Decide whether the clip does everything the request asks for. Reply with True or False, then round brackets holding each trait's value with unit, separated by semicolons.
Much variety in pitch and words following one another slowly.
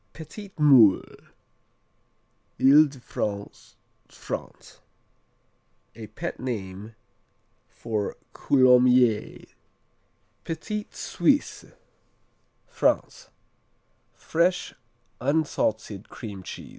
True (5.9 semitones; 65 wpm)